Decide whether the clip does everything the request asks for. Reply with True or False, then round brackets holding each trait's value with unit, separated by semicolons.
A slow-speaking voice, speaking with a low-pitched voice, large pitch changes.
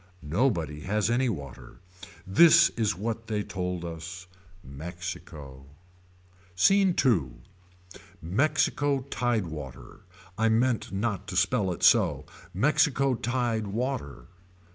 True (105 wpm; 100 Hz; 6.4 semitones)